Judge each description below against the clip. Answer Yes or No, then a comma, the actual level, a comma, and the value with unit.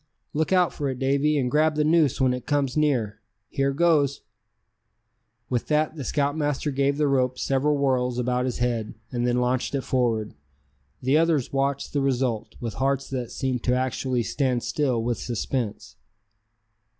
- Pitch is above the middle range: No, low, 135 Hz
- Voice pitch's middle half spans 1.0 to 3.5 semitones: Yes, average, 2.7 semitones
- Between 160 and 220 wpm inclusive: Yes, average, 165 wpm